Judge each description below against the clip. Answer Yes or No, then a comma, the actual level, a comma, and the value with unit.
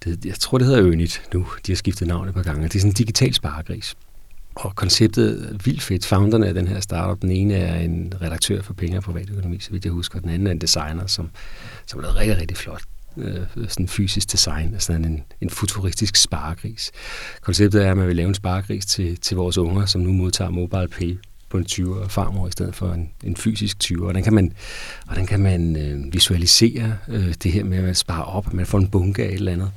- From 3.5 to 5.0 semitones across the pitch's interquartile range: No, average, 2.7 semitones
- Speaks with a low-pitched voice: Yes, very low, 95 Hz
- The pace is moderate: No, fast, 240 wpm